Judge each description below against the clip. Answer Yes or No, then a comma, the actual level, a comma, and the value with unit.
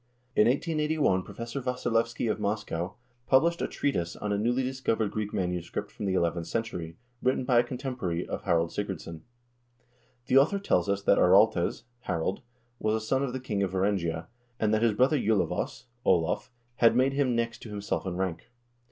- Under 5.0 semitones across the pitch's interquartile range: No, wide, 5.4 semitones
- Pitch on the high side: No, low, 110 Hz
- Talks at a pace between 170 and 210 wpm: Yes, average, 175 wpm